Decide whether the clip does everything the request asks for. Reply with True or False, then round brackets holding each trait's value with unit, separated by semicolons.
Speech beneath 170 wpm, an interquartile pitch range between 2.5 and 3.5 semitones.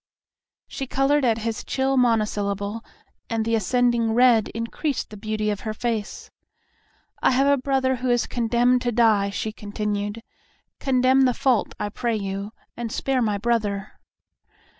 True (150 wpm; 3.0 semitones)